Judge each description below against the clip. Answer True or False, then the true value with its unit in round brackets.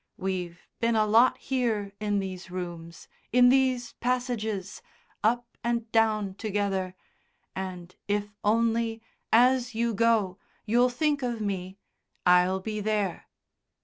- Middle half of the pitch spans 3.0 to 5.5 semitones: True (3.7 semitones)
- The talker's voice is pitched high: True (215 Hz)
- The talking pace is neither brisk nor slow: False (120 wpm)